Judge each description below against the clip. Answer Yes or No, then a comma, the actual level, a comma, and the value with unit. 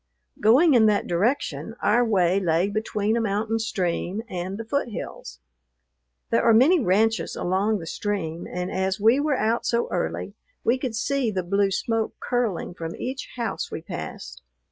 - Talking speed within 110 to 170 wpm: Yes, average, 165 wpm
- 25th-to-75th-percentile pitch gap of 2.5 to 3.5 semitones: No, average, 3.9 semitones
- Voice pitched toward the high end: Yes, high, 215 Hz